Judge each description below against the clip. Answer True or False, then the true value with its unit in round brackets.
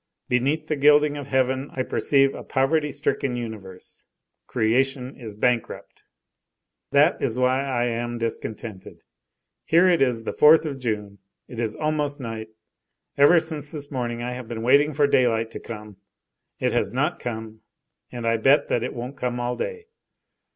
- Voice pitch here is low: True (125 Hz)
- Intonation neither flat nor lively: True (3.8 semitones)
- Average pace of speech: True (165 wpm)